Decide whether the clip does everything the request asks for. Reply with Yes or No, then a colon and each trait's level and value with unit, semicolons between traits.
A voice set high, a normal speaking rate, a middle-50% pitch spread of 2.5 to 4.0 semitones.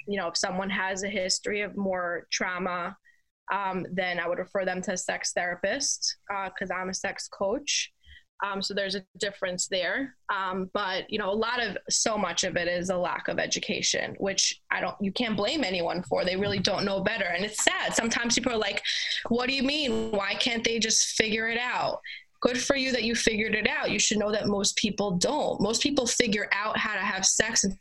No: high, 205 Hz; fast, 220 wpm; average, 3.4 semitones